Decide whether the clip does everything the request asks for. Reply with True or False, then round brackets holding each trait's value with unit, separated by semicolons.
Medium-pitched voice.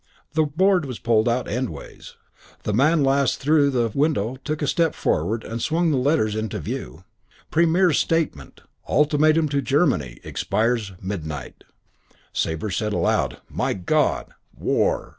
False (130 Hz)